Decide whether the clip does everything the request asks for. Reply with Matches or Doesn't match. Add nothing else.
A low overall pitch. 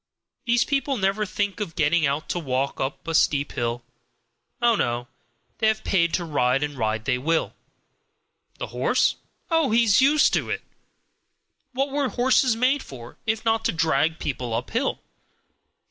Doesn't match